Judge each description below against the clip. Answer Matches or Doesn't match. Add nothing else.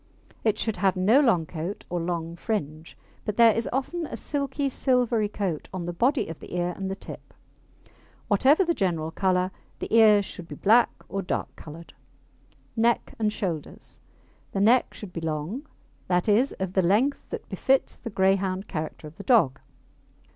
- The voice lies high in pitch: Matches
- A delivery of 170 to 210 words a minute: Matches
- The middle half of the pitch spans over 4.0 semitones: Matches